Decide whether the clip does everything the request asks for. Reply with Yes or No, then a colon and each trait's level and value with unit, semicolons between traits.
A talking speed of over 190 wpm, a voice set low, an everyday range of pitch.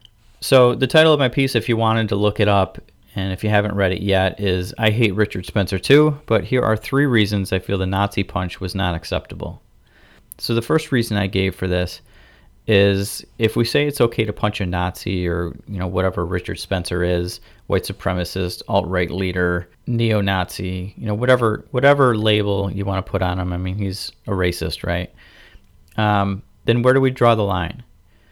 Yes: average, 200 wpm; low, 100 Hz; average, 3.4 semitones